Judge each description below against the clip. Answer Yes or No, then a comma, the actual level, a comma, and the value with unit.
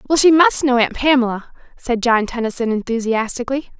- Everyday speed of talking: Yes, average, 160 wpm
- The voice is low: No, high, 245 Hz